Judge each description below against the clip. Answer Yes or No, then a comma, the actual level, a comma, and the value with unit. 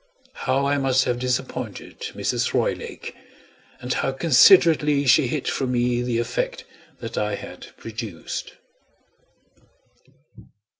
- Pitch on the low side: Yes, low, 125 Hz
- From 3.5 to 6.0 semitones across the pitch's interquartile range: No, narrow, 2.5 semitones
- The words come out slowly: Yes, slow, 110 wpm